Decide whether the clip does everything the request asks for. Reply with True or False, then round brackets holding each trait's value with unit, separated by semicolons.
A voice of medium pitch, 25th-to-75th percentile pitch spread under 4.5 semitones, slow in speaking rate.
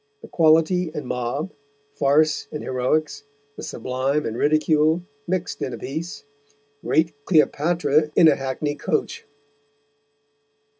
True (150 Hz; 2.5 semitones; 115 wpm)